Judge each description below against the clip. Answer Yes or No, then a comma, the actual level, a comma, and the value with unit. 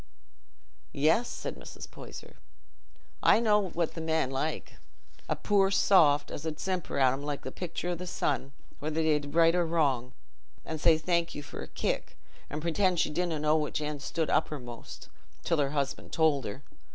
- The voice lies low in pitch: No, medium, 155 Hz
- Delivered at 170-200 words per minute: Yes, average, 180 wpm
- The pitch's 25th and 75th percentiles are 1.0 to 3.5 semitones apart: Yes, average, 2.9 semitones